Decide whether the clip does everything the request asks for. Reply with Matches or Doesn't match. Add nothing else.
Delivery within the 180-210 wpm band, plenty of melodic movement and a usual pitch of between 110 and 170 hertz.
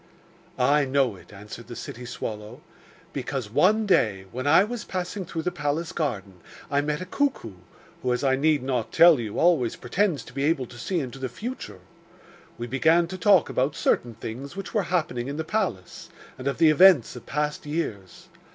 Matches